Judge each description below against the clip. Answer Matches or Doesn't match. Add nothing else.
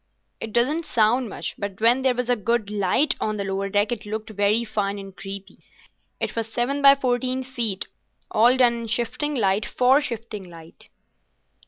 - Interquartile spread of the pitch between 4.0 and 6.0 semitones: Doesn't match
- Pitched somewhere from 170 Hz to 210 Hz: Doesn't match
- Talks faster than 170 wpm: Matches